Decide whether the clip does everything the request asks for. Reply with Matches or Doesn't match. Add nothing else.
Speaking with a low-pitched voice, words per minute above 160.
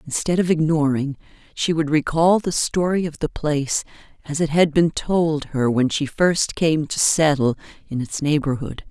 Doesn't match